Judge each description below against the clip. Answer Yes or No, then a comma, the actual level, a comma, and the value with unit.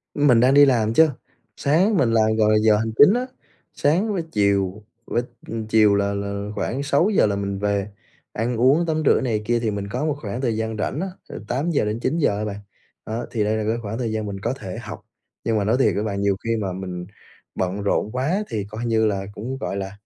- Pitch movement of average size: Yes, average, 4.2 semitones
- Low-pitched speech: Yes, low, 110 Hz